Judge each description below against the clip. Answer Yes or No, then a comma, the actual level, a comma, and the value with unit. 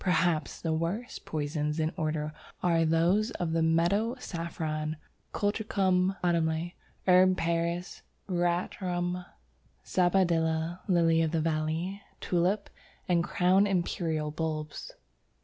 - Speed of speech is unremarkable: No, slow, 110 wpm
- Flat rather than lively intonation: Yes, narrow, 2.3 semitones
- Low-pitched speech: No, medium, 170 Hz